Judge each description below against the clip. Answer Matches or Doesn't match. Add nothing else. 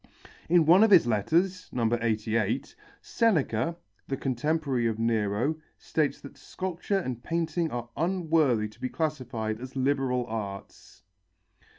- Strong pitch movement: Matches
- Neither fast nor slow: Doesn't match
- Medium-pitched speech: Doesn't match